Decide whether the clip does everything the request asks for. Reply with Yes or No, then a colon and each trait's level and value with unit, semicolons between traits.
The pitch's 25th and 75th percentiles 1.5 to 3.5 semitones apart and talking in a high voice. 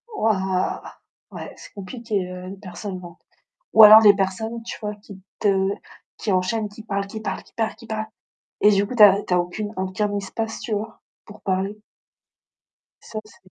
Yes: narrow, 2.4 semitones; high, 205 Hz